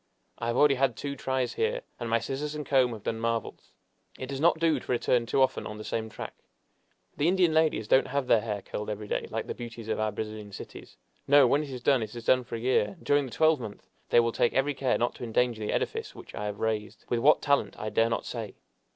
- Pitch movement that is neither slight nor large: Yes, average, 4.0 semitones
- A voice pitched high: No, low, 120 Hz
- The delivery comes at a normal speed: No, fast, 250 wpm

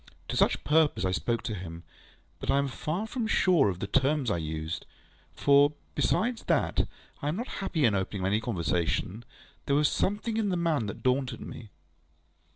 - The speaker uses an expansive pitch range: Yes, wide, 8.5 semitones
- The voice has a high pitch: No, low, 135 Hz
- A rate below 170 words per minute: No, average, 180 wpm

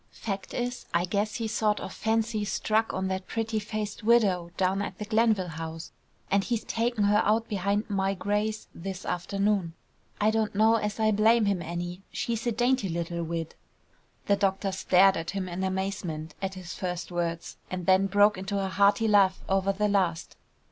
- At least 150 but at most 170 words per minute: No, average, 185 wpm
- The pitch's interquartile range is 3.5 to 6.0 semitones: No, average, 2.7 semitones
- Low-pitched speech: No, high, 200 Hz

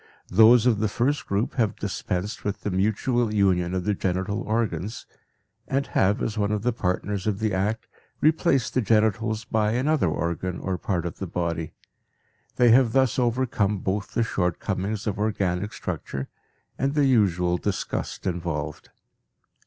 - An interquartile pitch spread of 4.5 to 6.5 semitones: No, average, 3.6 semitones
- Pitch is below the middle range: Yes, low, 105 Hz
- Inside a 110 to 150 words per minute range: No, average, 160 wpm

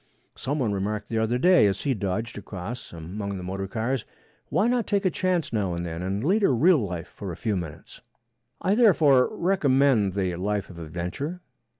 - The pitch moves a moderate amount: No, wide, 7.5 semitones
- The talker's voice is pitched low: Yes, low, 110 Hz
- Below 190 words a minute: No, average, 195 wpm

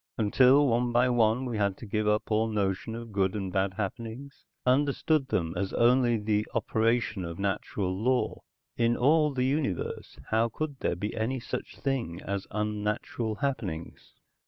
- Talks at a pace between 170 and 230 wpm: No, average, 160 wpm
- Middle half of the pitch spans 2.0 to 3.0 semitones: No, average, 3.8 semitones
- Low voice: Yes, low, 110 Hz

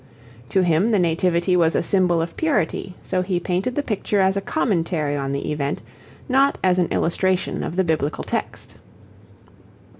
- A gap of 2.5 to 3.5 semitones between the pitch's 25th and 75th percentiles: Yes, average, 2.9 semitones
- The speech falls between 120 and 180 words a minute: Yes, average, 170 wpm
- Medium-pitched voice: Yes, medium, 180 Hz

